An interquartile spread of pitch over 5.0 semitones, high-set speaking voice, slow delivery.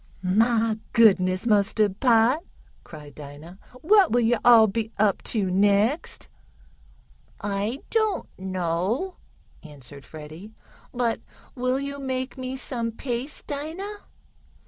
Yes: wide, 5.5 semitones; high, 225 Hz; slow, 110 wpm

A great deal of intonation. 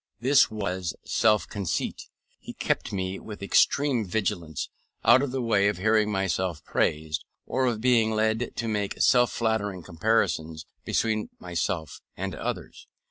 No: average, 3.5 semitones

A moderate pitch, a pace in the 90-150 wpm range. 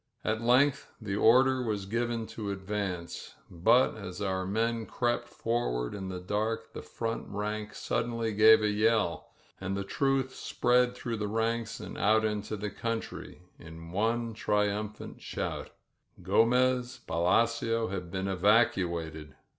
No: low, 110 Hz; average, 140 wpm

